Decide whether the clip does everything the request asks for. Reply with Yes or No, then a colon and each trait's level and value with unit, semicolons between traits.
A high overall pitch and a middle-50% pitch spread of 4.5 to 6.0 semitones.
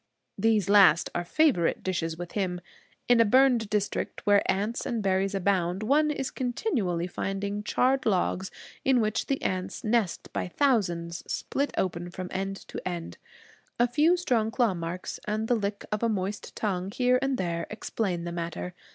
Yes: high, 200 Hz; average, 4.8 semitones